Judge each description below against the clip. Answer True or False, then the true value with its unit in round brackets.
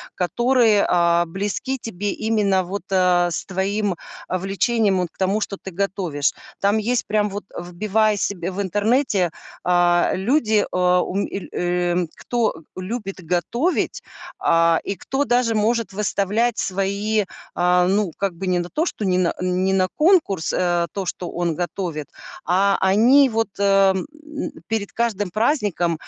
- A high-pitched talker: True (195 Hz)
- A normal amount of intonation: True (3.2 semitones)